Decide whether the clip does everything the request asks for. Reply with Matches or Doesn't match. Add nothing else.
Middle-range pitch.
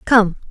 Doesn't match